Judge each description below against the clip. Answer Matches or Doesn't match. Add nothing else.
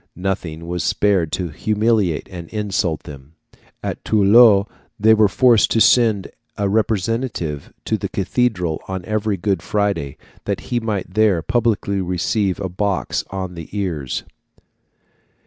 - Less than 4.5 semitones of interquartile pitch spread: Matches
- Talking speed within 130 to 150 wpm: Matches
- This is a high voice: Doesn't match